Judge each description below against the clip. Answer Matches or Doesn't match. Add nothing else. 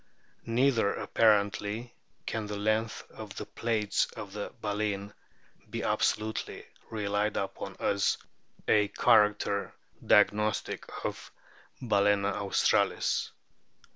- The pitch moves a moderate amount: Doesn't match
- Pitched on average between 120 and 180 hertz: Doesn't match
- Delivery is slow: Matches